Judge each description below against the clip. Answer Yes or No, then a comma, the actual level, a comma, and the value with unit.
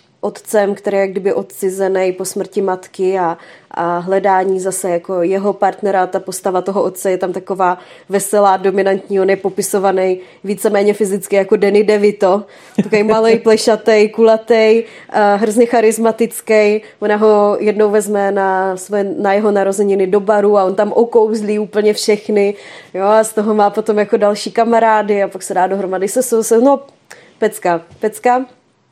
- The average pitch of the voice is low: No, high, 205 Hz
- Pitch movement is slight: Yes, narrow, 2.0 semitones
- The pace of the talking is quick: No, average, 160 wpm